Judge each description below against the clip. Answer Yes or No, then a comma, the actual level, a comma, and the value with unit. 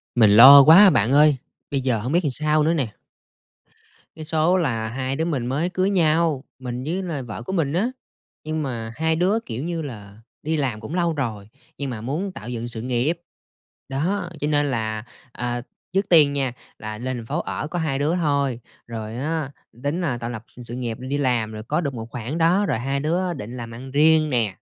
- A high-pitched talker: No, medium, 140 Hz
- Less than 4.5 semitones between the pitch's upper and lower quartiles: No, average, 5.1 semitones